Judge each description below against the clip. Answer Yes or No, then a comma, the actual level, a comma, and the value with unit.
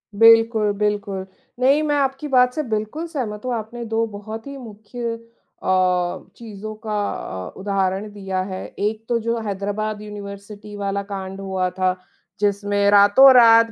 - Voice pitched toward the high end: Yes, high, 210 Hz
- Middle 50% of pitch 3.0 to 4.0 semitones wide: No, narrow, 2.4 semitones